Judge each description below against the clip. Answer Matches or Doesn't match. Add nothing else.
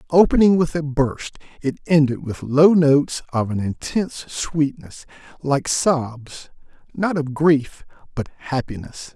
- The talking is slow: Matches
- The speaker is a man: Matches